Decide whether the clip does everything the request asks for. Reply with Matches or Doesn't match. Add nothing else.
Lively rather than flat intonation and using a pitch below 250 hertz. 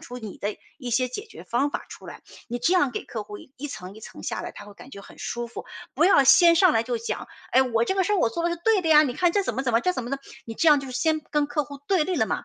Doesn't match